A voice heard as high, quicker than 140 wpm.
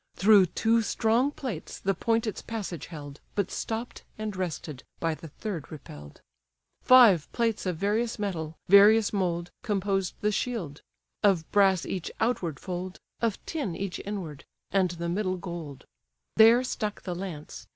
Yes: high, 195 Hz; average, 150 wpm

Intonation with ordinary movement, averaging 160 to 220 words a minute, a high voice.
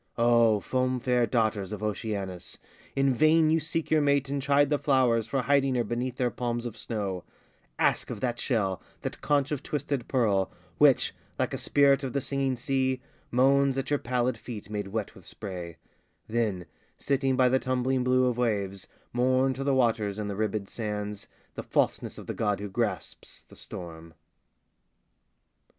No: average, 4.3 semitones; average, 175 wpm; low, 125 Hz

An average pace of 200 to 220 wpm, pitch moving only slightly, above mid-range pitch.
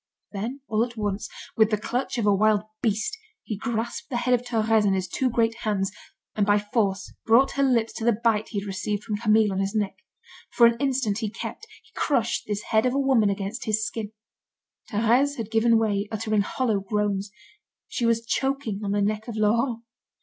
Yes: fast, 205 wpm; narrow, 2.3 semitones; high, 220 Hz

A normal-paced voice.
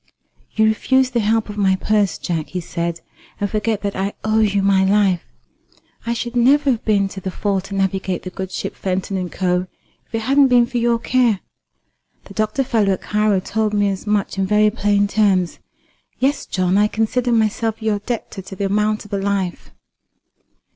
Yes: average, 195 wpm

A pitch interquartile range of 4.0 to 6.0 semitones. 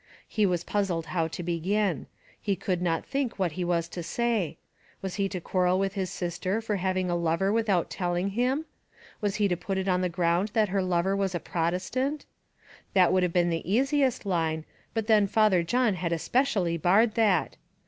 No: average, 3.3 semitones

